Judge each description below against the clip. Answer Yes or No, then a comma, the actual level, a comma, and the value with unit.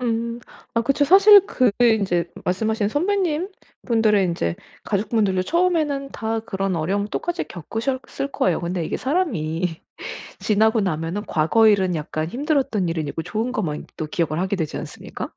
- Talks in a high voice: Yes, high, 215 Hz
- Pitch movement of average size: No, wide, 6.8 semitones